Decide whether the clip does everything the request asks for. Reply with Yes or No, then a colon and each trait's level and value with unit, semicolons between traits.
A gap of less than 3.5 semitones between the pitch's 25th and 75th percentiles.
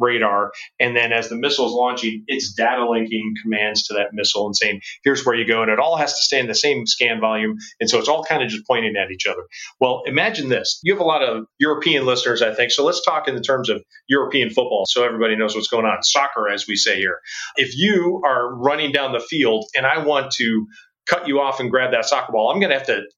No: average, 4.2 semitones